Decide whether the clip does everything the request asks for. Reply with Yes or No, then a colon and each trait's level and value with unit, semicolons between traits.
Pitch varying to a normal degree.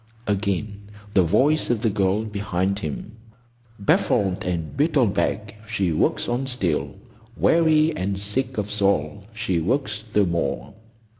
Yes: average, 3.2 semitones